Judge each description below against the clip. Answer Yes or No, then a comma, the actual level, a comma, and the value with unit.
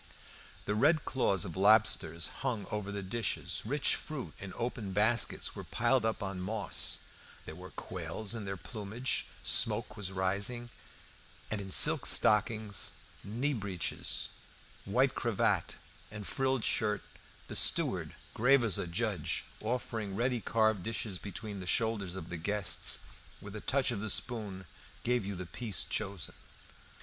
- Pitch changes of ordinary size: Yes, average, 3.3 semitones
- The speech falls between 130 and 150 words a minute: Yes, average, 145 wpm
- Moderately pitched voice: No, low, 105 Hz